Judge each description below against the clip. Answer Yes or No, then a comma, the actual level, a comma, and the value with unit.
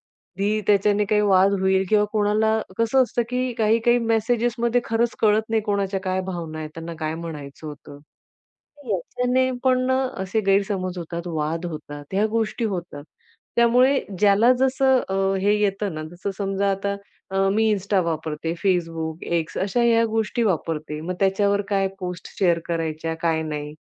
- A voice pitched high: Yes, high, 195 Hz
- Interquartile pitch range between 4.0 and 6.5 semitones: Yes, average, 4.6 semitones